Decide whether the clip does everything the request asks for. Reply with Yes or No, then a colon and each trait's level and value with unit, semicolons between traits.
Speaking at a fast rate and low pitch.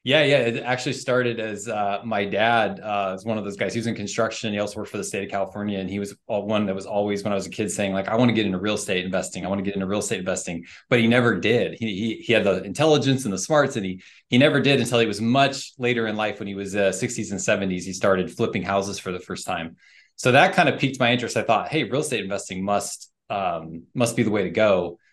Yes: fast, 280 wpm; low, 105 Hz